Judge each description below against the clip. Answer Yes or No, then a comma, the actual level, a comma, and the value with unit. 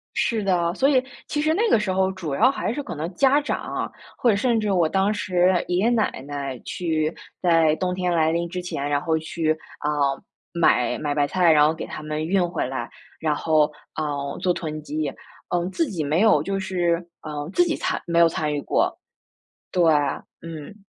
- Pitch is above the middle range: No, medium, 170 Hz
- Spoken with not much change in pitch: No, average, 4.0 semitones